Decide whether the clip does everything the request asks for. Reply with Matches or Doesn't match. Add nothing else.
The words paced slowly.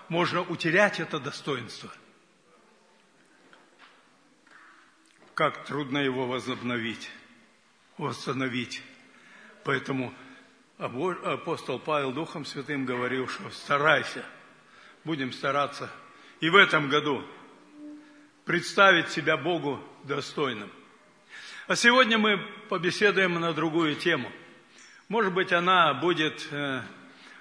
Matches